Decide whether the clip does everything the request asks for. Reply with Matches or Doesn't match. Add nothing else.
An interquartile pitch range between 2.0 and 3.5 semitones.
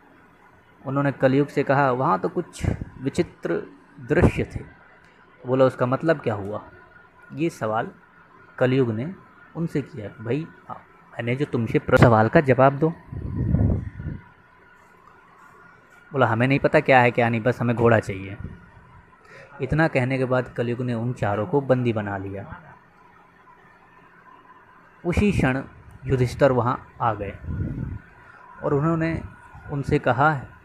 Doesn't match